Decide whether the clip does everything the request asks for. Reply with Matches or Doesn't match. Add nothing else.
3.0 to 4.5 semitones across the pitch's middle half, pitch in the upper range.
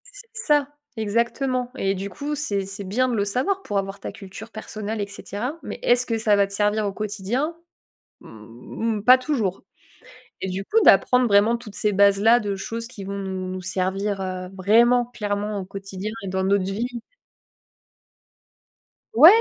Matches